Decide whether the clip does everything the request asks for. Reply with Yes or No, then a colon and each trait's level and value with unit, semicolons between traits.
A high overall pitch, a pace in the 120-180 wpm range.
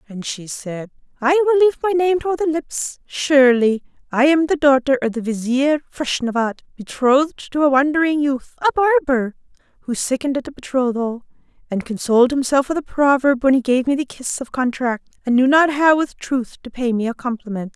No: very high, 265 Hz; average, 190 wpm